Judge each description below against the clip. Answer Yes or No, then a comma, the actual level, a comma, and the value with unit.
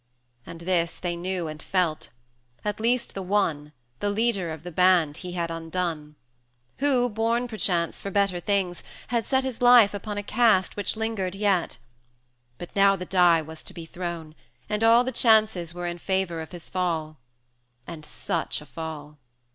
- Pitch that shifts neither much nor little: Yes, average, 3.9 semitones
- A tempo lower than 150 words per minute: No, average, 175 wpm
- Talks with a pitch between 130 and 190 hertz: Yes, medium, 185 Hz